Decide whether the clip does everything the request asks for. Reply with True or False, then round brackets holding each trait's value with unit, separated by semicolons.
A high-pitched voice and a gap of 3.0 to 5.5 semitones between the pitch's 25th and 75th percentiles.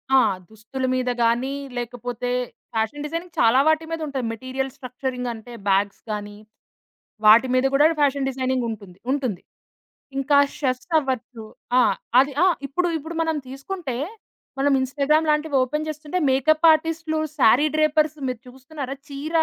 True (270 Hz; 3.8 semitones)